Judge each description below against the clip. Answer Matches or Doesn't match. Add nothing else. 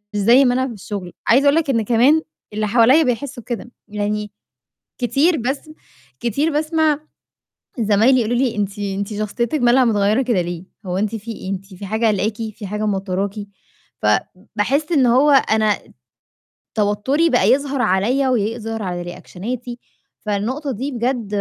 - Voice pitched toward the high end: Matches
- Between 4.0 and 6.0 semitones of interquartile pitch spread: Matches